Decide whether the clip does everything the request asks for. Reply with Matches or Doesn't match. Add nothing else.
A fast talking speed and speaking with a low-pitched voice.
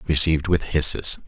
Doesn't match